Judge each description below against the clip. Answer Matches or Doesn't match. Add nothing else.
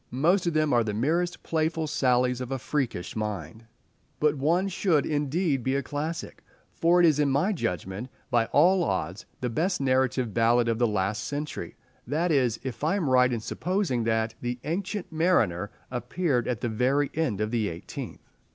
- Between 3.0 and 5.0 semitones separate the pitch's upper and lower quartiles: Doesn't match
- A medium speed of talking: Matches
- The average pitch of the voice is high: Doesn't match